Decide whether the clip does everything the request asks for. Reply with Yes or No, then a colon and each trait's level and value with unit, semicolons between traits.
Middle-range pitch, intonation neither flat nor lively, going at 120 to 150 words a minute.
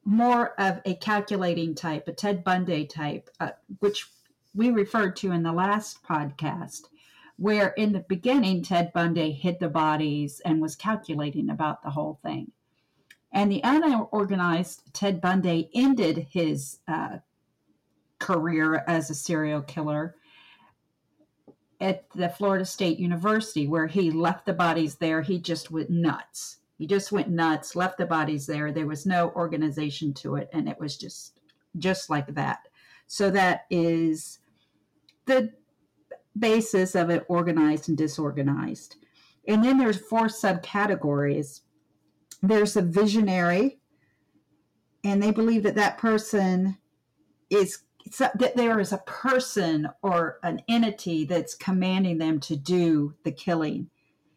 Yes: medium, 175 Hz; average, 4.5 semitones; slow, 135 wpm